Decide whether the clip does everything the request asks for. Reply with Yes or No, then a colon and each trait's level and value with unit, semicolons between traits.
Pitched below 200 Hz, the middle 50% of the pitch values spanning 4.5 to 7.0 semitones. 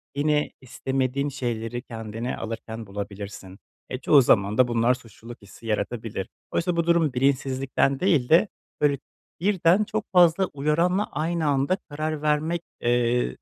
Yes: low, 135 Hz; average, 5.3 semitones